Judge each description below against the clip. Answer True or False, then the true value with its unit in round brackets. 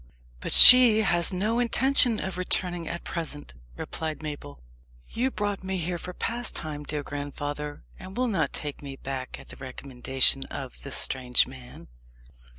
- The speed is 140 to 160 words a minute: True (155 wpm)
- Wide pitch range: True (5.8 semitones)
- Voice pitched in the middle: True (160 Hz)